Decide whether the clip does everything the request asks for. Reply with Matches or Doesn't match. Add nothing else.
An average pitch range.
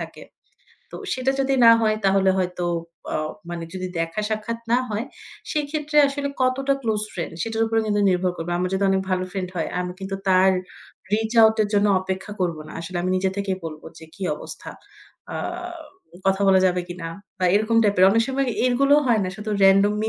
Matches